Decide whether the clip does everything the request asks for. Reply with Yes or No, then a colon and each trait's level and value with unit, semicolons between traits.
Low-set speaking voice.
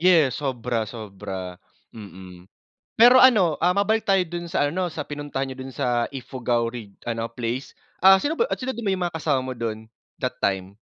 Yes: low, 130 Hz